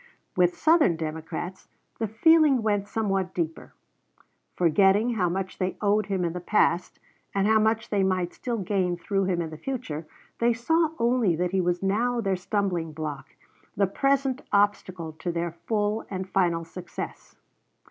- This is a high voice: Yes, high, 195 Hz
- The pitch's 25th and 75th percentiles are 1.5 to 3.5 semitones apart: No, average, 3.9 semitones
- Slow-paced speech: No, average, 160 wpm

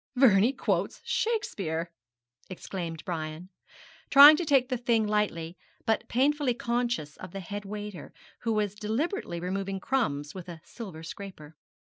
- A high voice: Yes, high, 205 Hz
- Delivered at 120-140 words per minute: Yes, slow, 135 wpm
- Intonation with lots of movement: Yes, wide, 6.1 semitones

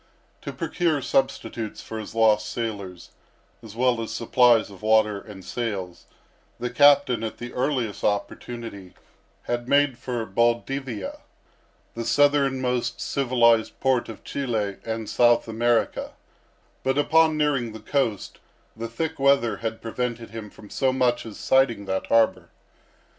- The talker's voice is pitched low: Yes, low, 115 Hz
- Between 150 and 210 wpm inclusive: No, slow, 135 wpm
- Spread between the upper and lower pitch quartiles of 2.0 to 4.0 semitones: Yes, average, 3.1 semitones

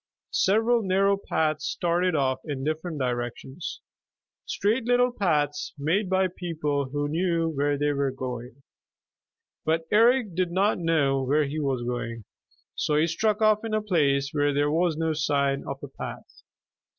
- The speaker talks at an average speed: Yes, average, 155 wpm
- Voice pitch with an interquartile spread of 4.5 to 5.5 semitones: Yes, average, 5.0 semitones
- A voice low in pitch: No, medium, 155 Hz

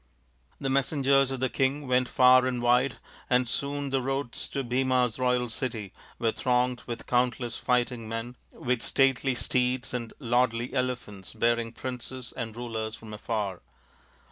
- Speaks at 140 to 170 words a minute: Yes, average, 145 wpm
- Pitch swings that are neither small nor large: No, narrow, 1.8 semitones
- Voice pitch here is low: Yes, low, 125 Hz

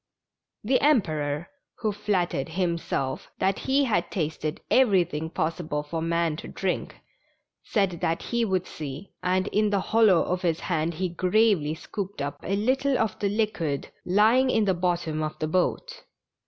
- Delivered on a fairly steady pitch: No, average, 4.7 semitones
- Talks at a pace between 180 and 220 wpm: No, average, 155 wpm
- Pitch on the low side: No, medium, 180 Hz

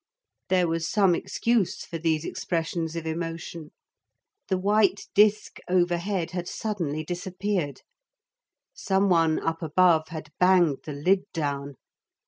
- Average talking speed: No, slow, 120 wpm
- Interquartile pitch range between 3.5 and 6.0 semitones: No, average, 2.8 semitones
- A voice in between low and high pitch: Yes, medium, 175 Hz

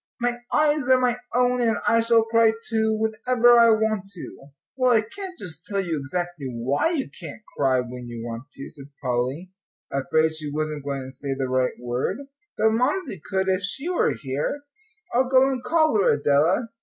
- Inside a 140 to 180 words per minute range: No, average, 190 wpm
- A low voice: No, high, 195 Hz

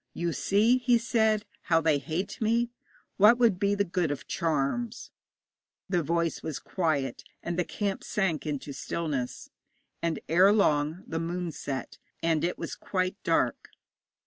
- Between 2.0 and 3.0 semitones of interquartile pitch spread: No, average, 4.5 semitones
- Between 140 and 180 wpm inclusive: Yes, average, 150 wpm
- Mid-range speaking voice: Yes, medium, 175 Hz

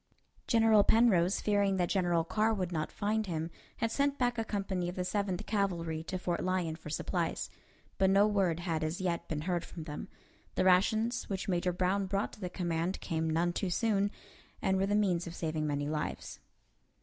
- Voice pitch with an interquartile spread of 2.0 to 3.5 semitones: Yes, average, 3.2 semitones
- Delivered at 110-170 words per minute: No, average, 195 wpm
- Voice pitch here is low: No, medium, 185 Hz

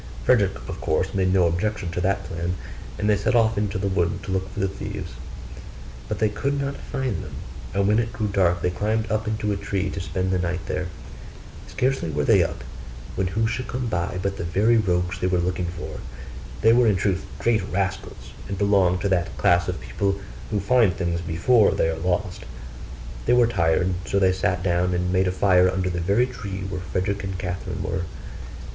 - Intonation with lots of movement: No, average, 2.8 semitones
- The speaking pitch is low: Yes, very low, 95 Hz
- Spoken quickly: Yes, fast, 210 wpm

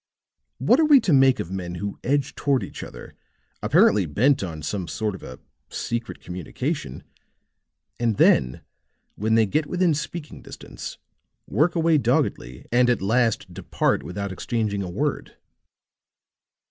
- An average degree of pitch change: No, wide, 7.1 semitones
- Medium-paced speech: Yes, average, 145 wpm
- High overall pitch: No, low, 115 Hz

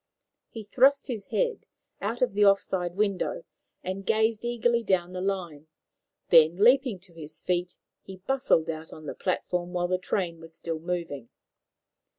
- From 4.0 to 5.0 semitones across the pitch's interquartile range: Yes, average, 4.4 semitones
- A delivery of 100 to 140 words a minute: No, average, 165 wpm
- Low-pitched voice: No, medium, 185 Hz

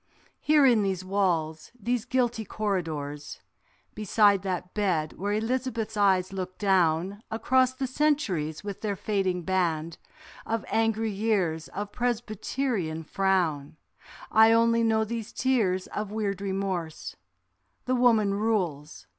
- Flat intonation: No, average, 3.7 semitones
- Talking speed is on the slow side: Yes, slow, 120 wpm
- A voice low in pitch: No, high, 200 Hz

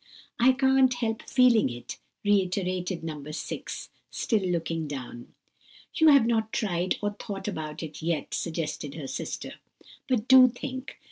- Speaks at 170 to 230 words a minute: No, average, 140 wpm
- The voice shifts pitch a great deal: Yes, wide, 7.1 semitones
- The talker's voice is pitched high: Yes, high, 195 Hz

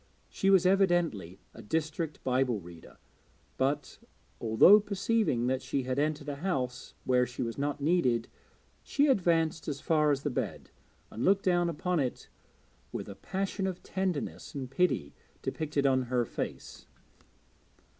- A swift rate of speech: No, average, 145 wpm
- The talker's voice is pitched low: No, medium, 150 Hz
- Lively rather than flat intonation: Yes, wide, 5.9 semitones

